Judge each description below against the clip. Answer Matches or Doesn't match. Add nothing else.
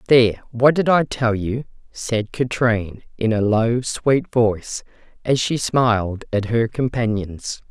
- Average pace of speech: Matches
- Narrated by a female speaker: Matches